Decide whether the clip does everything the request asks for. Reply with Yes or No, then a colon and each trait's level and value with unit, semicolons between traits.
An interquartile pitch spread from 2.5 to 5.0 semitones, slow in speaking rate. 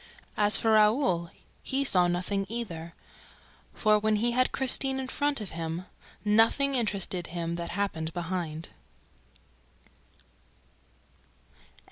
No: wide, 5.5 semitones; slow, 110 wpm